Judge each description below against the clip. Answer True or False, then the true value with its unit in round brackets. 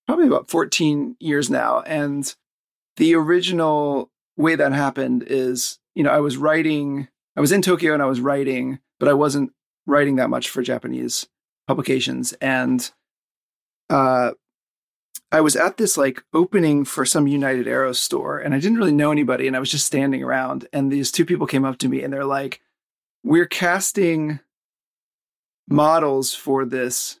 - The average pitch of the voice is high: False (140 Hz)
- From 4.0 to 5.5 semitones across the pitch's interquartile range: False (2.6 semitones)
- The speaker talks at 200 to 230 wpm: False (165 wpm)